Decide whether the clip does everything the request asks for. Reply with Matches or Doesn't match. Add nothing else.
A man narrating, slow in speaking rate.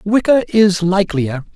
Matches